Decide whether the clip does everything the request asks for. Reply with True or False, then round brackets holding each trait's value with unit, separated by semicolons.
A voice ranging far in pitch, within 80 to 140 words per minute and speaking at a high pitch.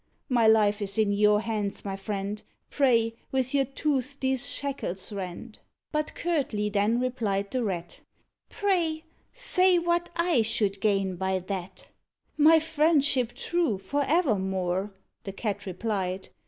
True (6.2 semitones; 135 wpm; 225 Hz)